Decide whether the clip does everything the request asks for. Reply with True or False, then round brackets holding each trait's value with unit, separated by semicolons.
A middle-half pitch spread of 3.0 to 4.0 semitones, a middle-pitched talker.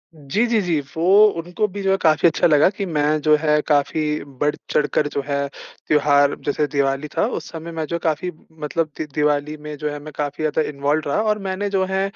False (2.4 semitones; 150 Hz)